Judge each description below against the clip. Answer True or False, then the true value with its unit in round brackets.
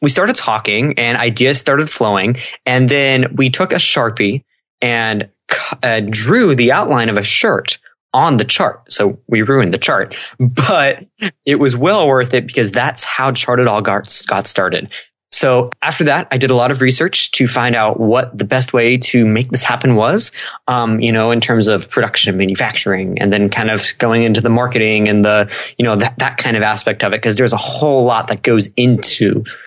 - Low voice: True (120 Hz)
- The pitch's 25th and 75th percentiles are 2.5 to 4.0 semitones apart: True (2.9 semitones)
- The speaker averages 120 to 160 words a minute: False (200 wpm)